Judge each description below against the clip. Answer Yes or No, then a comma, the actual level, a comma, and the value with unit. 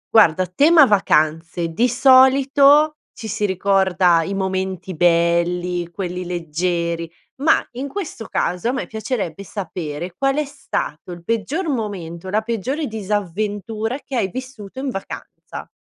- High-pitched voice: Yes, high, 200 Hz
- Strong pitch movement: Yes, wide, 6.7 semitones